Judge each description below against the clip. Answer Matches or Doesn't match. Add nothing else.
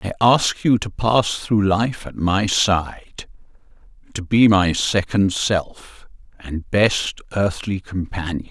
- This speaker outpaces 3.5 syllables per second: Doesn't match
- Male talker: Matches